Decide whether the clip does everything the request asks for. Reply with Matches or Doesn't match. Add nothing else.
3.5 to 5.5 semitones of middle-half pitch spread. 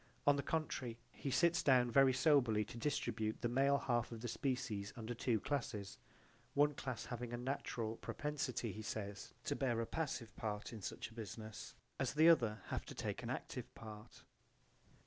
Matches